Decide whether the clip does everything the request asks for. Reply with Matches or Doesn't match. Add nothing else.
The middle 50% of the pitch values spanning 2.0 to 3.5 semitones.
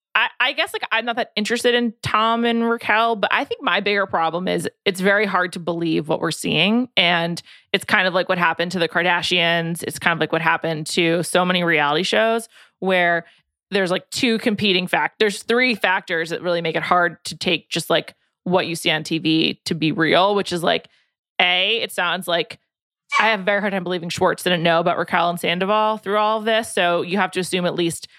Doesn't match